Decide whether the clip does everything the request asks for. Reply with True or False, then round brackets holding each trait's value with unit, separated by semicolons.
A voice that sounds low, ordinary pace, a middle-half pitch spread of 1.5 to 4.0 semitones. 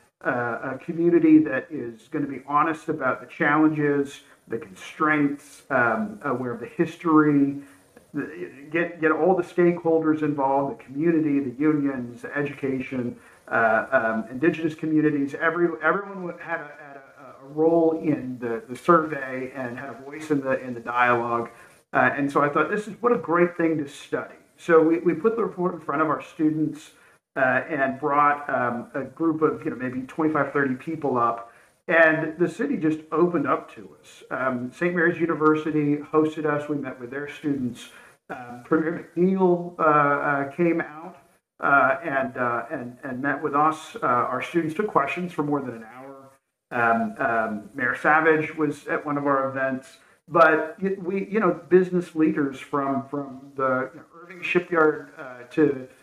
False (150 Hz; 175 wpm; 3.6 semitones)